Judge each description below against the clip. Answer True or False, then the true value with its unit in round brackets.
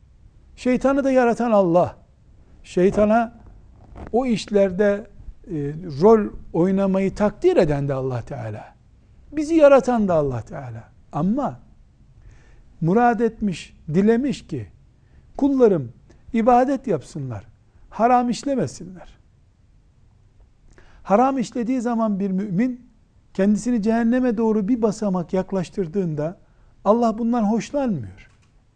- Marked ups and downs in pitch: True (8.8 semitones)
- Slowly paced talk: True (90 wpm)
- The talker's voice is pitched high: True (200 Hz)